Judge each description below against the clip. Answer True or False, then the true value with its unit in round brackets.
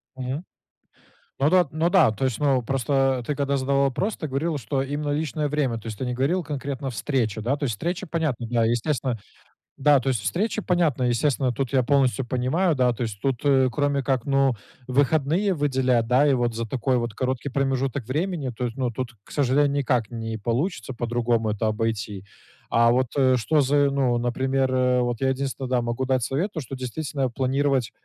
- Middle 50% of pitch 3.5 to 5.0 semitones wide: False (2.9 semitones)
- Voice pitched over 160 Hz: False (130 Hz)